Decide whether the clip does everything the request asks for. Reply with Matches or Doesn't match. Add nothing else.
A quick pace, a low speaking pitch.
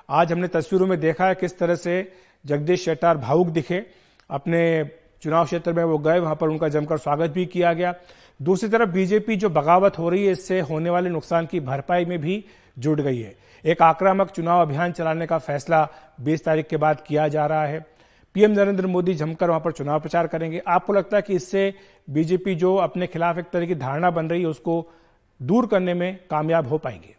Doesn't match